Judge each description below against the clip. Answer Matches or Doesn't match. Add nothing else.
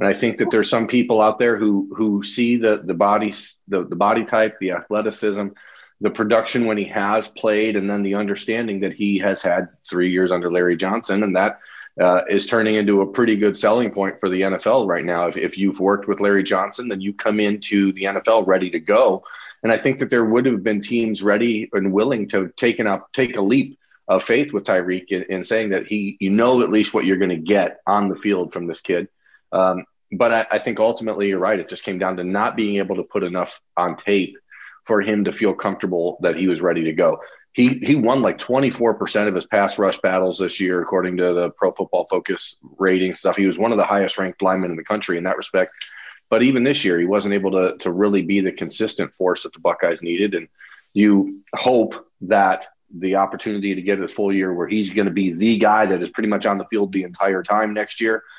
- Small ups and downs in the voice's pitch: Matches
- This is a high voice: Doesn't match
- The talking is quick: Matches